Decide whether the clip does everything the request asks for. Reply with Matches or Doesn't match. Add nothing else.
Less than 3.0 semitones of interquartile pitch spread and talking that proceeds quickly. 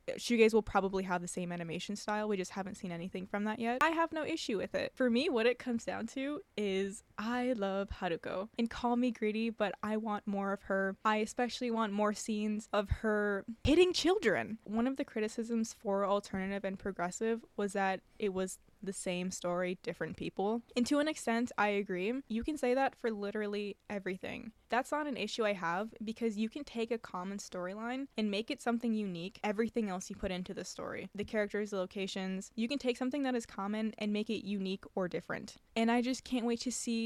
Doesn't match